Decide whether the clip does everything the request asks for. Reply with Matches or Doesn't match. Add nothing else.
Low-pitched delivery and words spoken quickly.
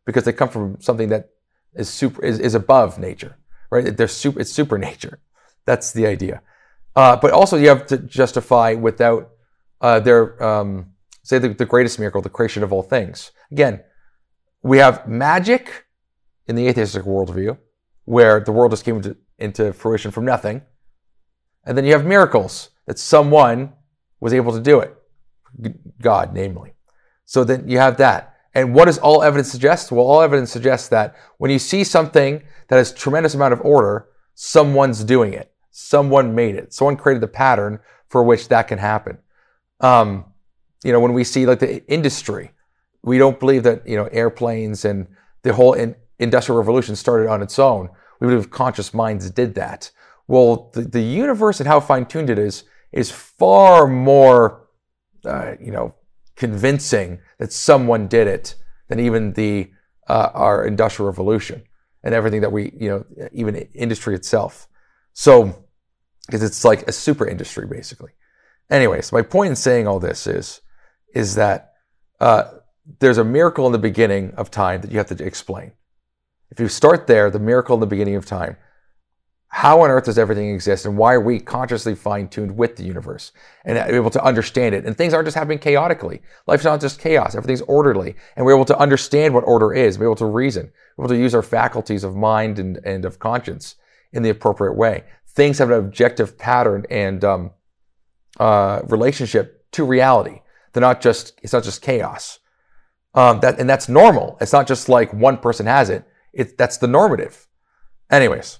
Doesn't match